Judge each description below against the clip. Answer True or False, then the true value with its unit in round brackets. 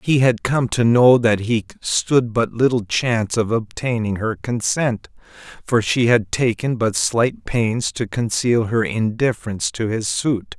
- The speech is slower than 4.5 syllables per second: True (4.1 syllables/s)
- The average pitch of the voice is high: False (115 Hz)